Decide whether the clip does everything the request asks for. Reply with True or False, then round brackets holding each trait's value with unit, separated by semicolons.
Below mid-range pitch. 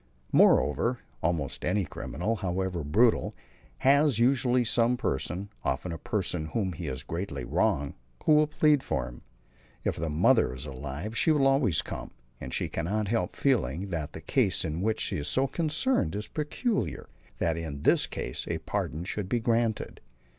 True (95 Hz)